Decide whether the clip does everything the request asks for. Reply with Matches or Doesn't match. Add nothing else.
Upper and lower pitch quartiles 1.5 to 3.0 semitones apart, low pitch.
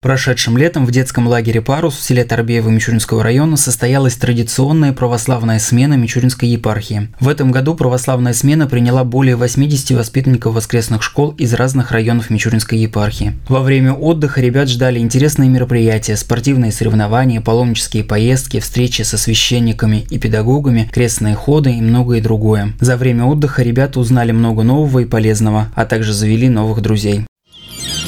Matches